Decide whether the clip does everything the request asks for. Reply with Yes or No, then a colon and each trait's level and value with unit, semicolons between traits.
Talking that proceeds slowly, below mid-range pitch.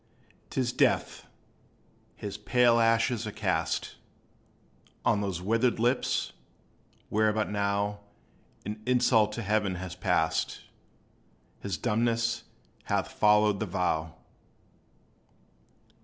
Yes: slow, 100 wpm; low, 105 Hz